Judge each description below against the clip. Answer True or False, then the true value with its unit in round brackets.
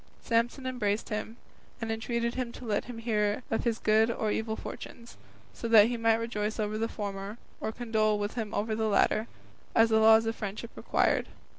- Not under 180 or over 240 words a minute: True (190 wpm)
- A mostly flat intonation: True (1.5 semitones)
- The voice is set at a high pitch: True (225 Hz)